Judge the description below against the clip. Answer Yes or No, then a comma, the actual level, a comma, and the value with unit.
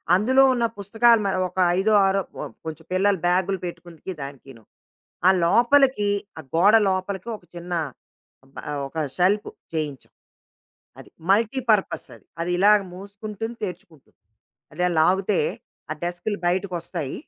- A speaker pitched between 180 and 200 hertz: Yes, high, 190 Hz